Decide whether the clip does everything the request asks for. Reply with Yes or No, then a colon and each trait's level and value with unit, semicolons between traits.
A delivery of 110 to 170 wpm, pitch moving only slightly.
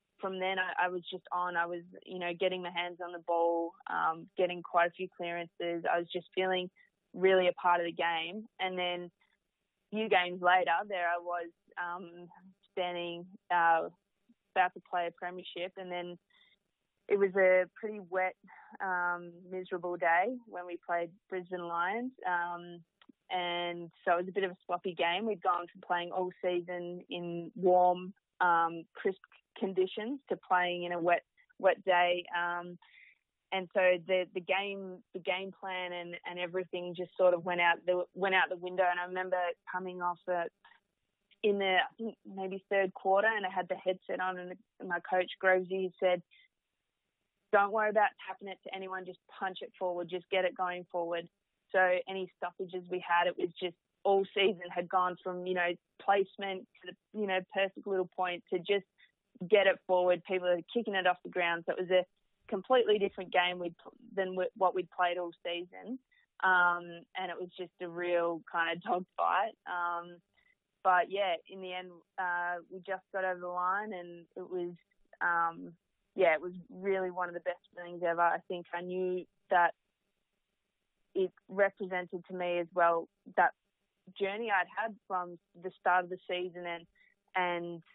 No: average, 185 wpm; narrow, 1.5 semitones